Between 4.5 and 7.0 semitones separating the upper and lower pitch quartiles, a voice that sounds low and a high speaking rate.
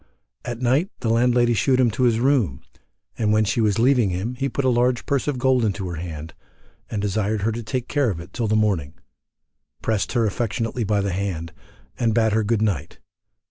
No: average, 3.5 semitones; low, 110 Hz; fast, 210 wpm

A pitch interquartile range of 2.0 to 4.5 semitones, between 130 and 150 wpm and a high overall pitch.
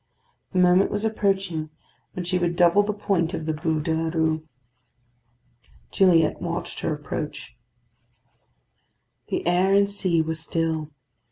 No: average, 3.1 semitones; average, 140 wpm; medium, 170 Hz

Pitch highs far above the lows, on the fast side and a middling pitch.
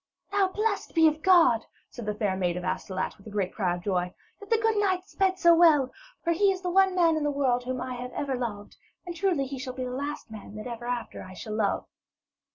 No: wide, 8.8 semitones; fast, 245 wpm; very high, 260 Hz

